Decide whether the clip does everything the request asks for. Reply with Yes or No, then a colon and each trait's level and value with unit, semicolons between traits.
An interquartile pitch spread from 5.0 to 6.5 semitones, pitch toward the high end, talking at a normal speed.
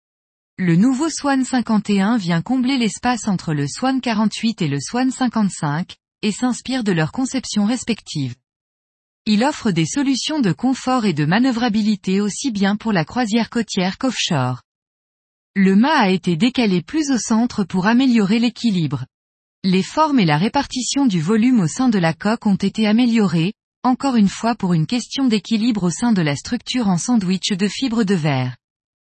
Yes: wide, 5.4 semitones; high, 215 Hz; average, 165 wpm